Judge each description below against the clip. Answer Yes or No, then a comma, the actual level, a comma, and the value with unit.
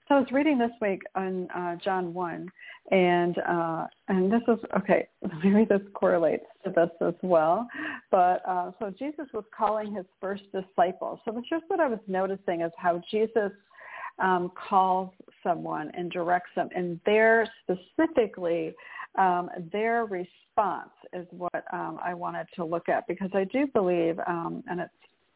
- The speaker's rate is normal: Yes, average, 165 wpm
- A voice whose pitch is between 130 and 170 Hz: No, high, 190 Hz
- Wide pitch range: No, average, 3.7 semitones